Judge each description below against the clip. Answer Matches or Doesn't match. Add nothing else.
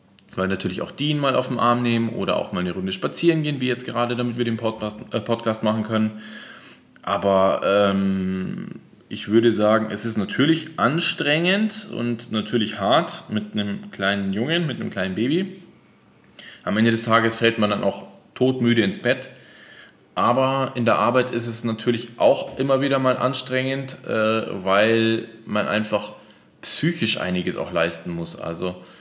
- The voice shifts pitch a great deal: Doesn't match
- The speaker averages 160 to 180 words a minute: Matches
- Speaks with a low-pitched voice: Matches